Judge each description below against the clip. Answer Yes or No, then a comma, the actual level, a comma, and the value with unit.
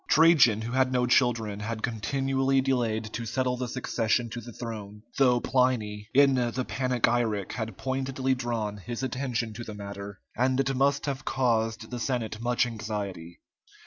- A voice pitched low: Yes, low, 120 Hz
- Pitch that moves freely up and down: No, average, 3.0 semitones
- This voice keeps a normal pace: Yes, average, 160 wpm